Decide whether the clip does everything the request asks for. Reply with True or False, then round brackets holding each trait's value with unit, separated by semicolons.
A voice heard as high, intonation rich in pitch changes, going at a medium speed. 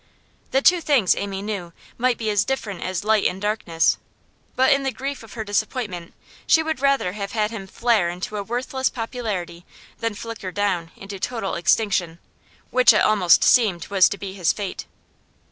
False (210 Hz; 4.2 semitones; 180 wpm)